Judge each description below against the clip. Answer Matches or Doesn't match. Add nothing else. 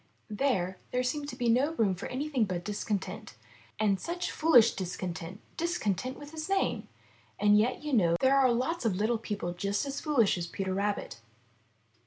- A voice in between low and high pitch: Doesn't match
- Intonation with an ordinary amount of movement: Doesn't match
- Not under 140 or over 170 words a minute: Doesn't match